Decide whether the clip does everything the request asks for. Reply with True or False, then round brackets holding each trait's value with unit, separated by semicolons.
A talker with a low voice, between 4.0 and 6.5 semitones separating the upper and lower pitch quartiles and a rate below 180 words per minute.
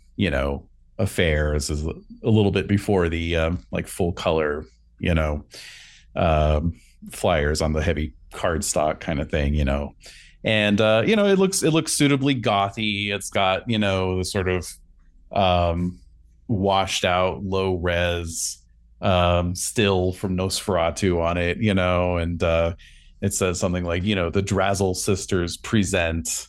False (90 Hz; 3.2 semitones; 155 wpm)